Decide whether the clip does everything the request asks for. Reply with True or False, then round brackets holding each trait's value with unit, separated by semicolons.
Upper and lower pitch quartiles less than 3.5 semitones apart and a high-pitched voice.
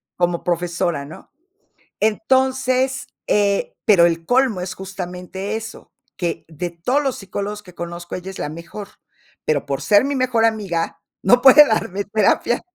False (5.2 semitones; 195 Hz)